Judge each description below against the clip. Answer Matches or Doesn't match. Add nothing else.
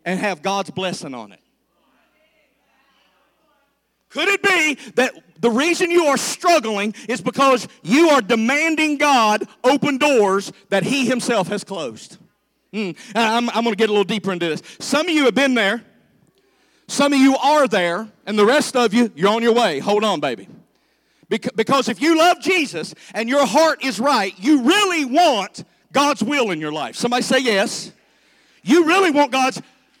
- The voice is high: Matches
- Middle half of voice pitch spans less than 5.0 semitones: Doesn't match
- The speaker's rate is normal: Matches